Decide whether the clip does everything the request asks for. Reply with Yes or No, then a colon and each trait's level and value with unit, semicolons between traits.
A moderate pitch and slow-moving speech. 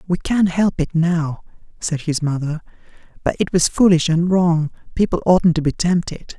No: medium, 170 Hz; average, 180 wpm